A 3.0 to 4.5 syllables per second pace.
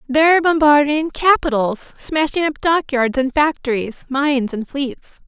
Yes: 4.4 syllables/s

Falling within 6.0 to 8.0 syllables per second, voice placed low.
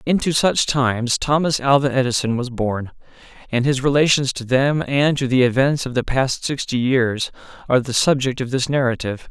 No: 5.2 syllables/s; low, 130 Hz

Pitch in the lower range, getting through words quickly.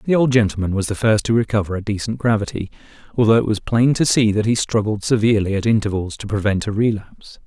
Yes: low, 110 Hz; fast, 215 wpm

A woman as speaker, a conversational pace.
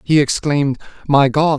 No: male; average, 150 wpm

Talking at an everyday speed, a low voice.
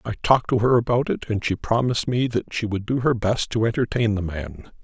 No: fast, 250 wpm; low, 115 Hz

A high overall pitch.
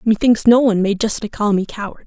Yes: high, 215 Hz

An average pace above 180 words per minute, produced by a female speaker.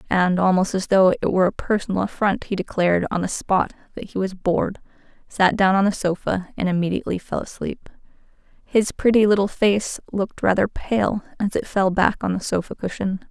Yes: average, 190 wpm; female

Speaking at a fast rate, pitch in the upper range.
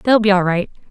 Yes: fast, 265 wpm; high, 200 Hz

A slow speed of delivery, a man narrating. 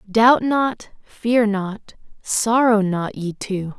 No: slow, 125 wpm; female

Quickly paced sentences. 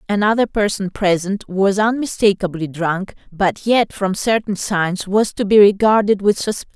No: average, 150 wpm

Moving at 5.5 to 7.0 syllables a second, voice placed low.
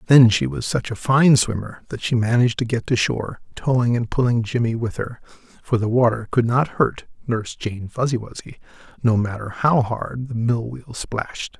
No: 5.1 syllables/s; low, 115 Hz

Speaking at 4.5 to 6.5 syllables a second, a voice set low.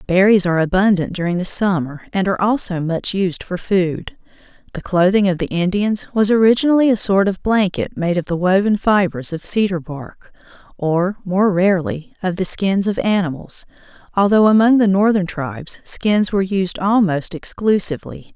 No: 5.0 syllables/s; high, 190 Hz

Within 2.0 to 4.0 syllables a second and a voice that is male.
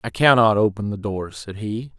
No: 4.9 syllables/s; male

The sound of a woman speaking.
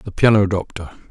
No: male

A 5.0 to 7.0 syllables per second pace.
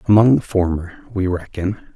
Yes: 5.1 syllables/s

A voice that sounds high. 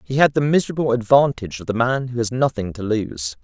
No: low, 120 Hz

